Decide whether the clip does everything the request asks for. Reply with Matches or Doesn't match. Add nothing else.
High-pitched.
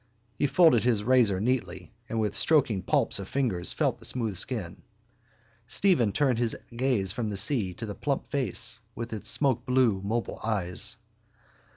Doesn't match